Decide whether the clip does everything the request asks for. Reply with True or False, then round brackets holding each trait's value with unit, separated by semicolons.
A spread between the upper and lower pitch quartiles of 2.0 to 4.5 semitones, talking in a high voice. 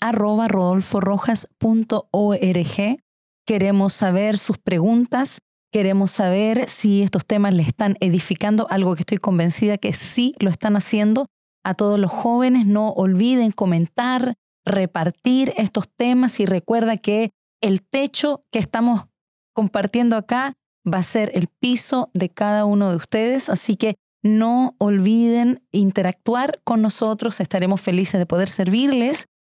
True (3.3 semitones; 210 Hz)